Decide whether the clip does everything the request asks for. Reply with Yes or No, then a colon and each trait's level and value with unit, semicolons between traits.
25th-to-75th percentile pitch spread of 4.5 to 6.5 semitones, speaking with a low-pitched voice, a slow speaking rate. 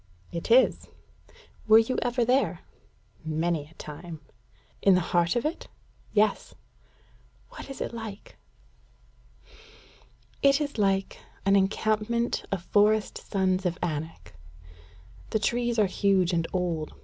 No: average, 5.1 semitones; high, 195 Hz; slow, 125 wpm